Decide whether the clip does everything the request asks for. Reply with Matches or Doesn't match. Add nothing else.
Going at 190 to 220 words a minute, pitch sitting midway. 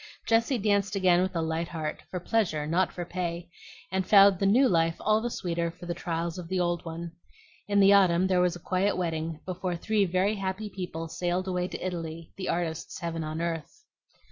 Matches